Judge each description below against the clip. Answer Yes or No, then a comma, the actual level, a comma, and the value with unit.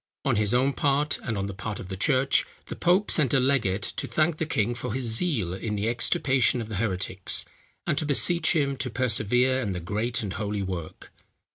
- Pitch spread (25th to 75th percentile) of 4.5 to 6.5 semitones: Yes, average, 5.1 semitones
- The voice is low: Yes, low, 120 Hz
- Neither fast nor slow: No, fast, 215 wpm